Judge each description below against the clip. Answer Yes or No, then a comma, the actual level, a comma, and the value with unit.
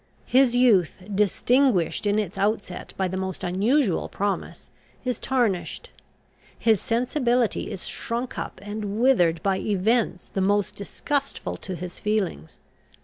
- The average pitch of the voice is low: No, high, 205 Hz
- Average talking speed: No, slow, 130 wpm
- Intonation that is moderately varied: Yes, average, 4.3 semitones